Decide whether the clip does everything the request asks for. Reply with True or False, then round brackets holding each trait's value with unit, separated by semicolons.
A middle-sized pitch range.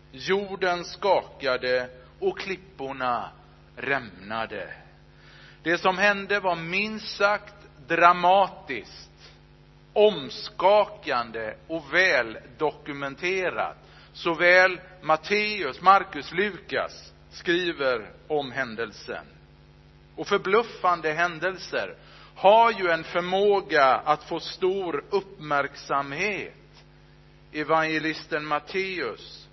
False (5.9 semitones)